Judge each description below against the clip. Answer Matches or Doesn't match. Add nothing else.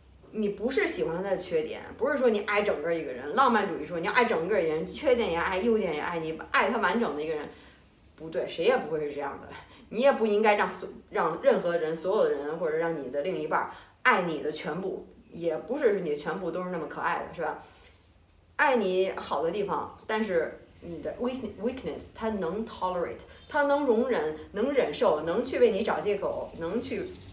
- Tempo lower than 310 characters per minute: Doesn't match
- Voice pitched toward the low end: Doesn't match